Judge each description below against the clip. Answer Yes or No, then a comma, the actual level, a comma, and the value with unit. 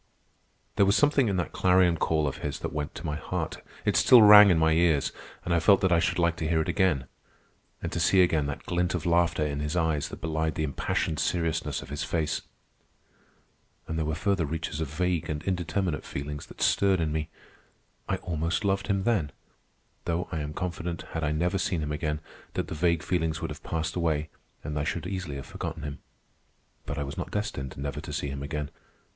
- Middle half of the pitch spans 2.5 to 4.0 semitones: Yes, average, 2.9 semitones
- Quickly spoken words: Yes, fast, 215 wpm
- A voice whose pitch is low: Yes, very low, 80 Hz